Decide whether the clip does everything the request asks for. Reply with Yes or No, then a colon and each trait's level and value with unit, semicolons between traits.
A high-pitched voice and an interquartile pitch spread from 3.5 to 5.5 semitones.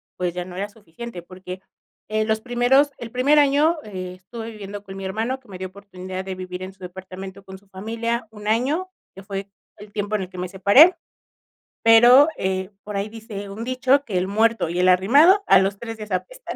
Yes: high, 205 Hz; average, 3.9 semitones